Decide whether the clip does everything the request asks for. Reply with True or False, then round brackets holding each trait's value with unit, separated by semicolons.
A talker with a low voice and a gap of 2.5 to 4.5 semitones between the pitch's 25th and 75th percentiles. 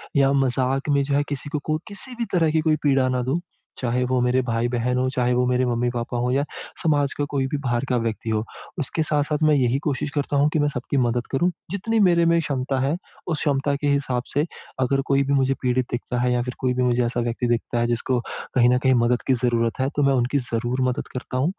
True (130 Hz; 2.8 semitones)